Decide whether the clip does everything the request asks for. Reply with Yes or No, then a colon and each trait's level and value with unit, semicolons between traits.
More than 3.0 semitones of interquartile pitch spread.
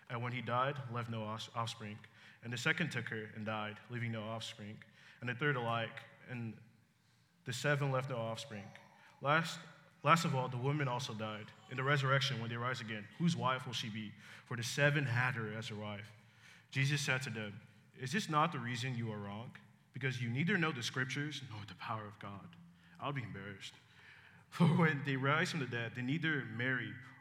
Yes: average, 4.2 semitones